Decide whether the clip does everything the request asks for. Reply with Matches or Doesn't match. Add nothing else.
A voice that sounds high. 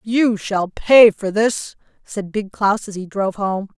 Matches